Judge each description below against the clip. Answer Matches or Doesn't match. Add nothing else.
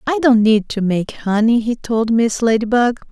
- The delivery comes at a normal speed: Matches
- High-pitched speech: Matches